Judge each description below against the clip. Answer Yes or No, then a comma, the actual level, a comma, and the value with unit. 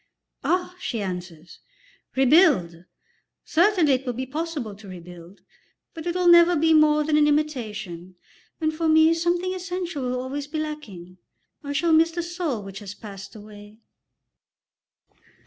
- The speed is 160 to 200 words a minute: No, average, 145 wpm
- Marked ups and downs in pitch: Yes, wide, 8.1 semitones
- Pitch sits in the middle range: No, very high, 290 Hz